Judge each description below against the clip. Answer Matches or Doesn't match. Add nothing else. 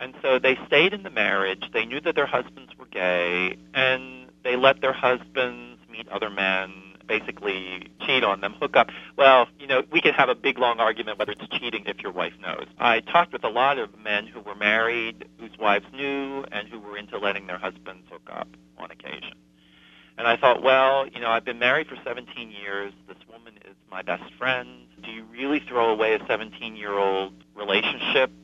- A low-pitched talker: Matches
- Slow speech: Doesn't match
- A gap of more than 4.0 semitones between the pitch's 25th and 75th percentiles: Matches